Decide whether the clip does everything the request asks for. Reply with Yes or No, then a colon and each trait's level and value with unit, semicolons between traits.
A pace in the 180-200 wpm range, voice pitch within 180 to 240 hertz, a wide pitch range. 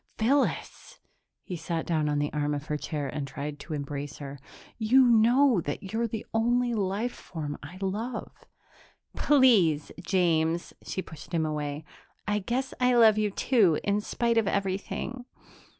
No: average, 160 wpm; high, 190 Hz; wide, 7.3 semitones